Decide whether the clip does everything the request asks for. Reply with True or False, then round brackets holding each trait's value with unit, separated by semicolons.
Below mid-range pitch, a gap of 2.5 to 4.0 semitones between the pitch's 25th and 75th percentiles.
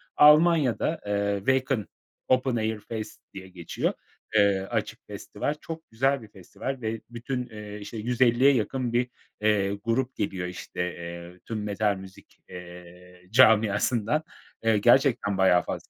False (110 Hz; 4.4 semitones)